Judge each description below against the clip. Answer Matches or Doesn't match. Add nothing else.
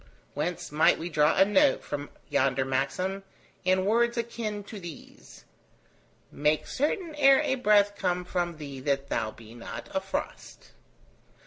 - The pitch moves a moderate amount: Doesn't match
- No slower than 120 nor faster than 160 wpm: Matches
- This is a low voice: Doesn't match